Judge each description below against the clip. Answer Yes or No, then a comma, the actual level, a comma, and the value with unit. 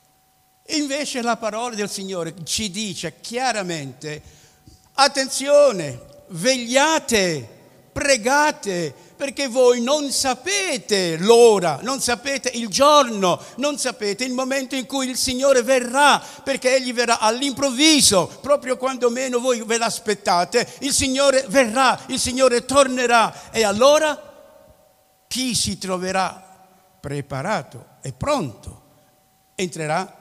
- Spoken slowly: Yes, slow, 105 wpm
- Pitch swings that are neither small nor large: No, wide, 6.3 semitones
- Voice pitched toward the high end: Yes, high, 245 Hz